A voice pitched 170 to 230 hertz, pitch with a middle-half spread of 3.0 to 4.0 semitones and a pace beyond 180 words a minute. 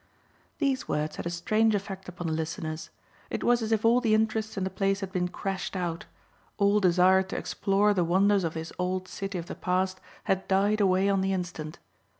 No: high, 190 Hz; narrow, 2.4 semitones; fast, 205 wpm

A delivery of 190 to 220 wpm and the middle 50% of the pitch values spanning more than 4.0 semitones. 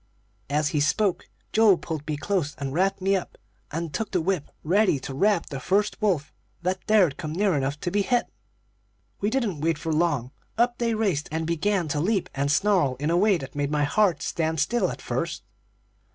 Yes: average, 195 wpm; wide, 5.5 semitones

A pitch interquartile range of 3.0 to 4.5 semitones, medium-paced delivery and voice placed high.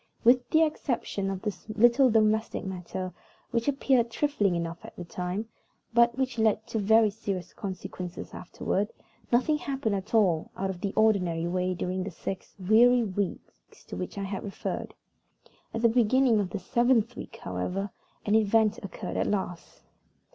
Yes: average, 4.0 semitones; average, 160 wpm; high, 210 Hz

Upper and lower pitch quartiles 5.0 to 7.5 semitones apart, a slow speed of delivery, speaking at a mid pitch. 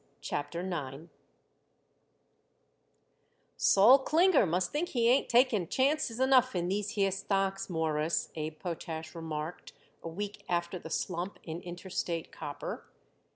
Yes: wide, 5.6 semitones; slow, 120 wpm; medium, 180 Hz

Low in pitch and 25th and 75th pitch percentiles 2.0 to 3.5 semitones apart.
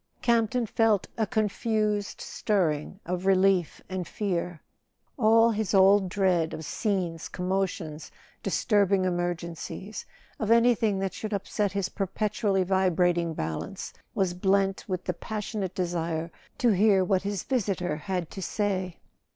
No: high, 190 Hz; average, 2.8 semitones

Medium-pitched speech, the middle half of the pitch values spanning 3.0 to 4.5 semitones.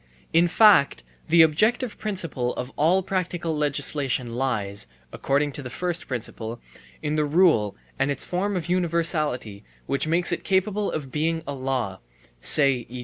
No: medium, 150 Hz; average, 5.3 semitones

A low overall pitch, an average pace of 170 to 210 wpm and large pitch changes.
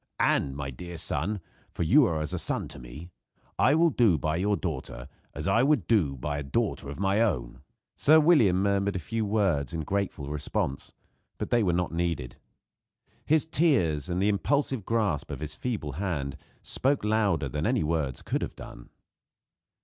Yes: very low, 90 Hz; average, 180 wpm; wide, 6.8 semitones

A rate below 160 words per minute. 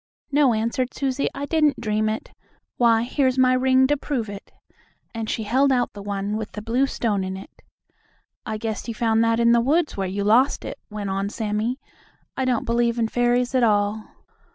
No: average, 200 wpm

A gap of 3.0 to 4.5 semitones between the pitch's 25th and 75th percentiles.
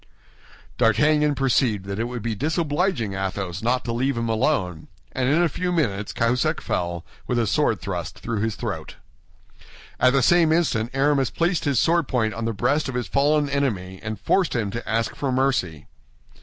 No: average, 5.0 semitones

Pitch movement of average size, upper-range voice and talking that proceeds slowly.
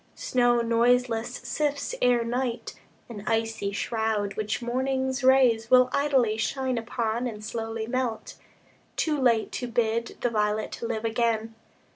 No: narrow, 2.2 semitones; high, 235 Hz; slow, 130 wpm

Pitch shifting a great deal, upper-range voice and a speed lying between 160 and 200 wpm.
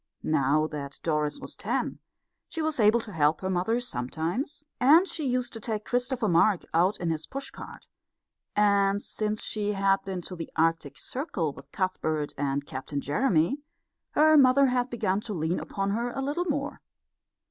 Yes: wide, 7.7 semitones; high, 200 Hz; average, 170 wpm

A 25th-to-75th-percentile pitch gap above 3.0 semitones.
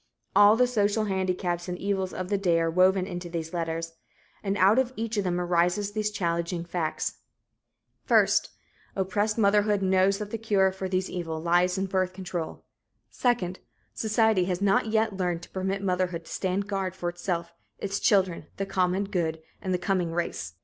No: narrow, 2.4 semitones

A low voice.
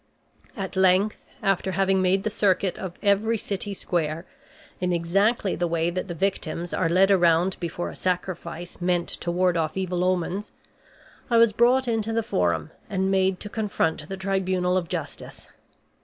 No: medium, 185 Hz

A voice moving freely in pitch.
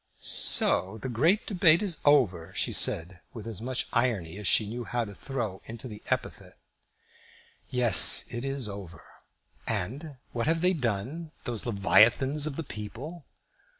Yes: wide, 5.7 semitones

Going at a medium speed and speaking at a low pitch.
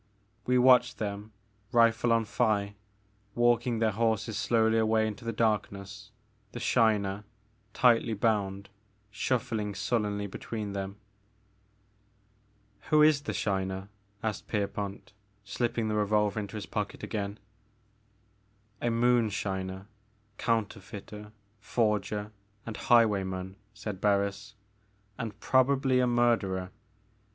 No: slow, 105 wpm; low, 105 Hz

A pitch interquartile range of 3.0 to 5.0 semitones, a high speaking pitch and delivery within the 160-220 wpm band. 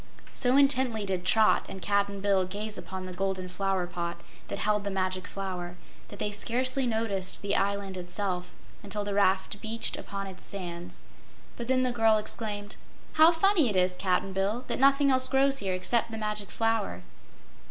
Yes: average, 3.3 semitones; high, 200 Hz; average, 175 wpm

